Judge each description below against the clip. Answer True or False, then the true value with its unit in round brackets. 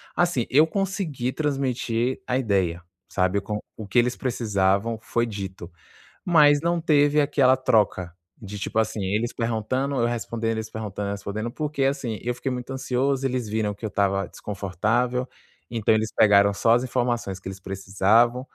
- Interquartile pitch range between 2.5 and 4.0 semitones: False (4.4 semitones)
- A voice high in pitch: False (115 Hz)